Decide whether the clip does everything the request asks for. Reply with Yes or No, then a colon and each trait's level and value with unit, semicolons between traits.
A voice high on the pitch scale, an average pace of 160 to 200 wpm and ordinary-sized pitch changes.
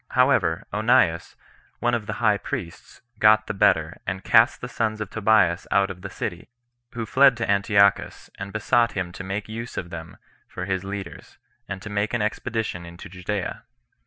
No: low, 105 Hz; average, 180 wpm; average, 3.0 semitones